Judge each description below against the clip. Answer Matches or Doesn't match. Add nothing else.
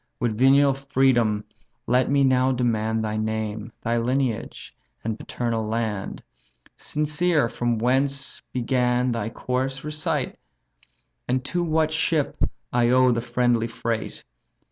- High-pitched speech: Doesn't match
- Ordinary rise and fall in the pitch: Matches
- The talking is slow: Matches